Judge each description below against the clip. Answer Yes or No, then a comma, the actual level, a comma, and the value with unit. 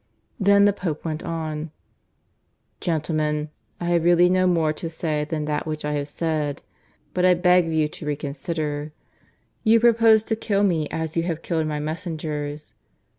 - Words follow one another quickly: No, average, 170 wpm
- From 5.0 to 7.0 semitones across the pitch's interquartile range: No, average, 2.9 semitones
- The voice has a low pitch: No, medium, 160 Hz